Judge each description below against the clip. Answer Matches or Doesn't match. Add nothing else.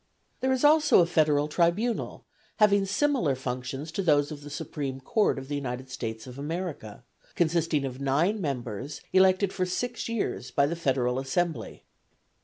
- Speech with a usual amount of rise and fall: Doesn't match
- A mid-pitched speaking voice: Matches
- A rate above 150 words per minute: Matches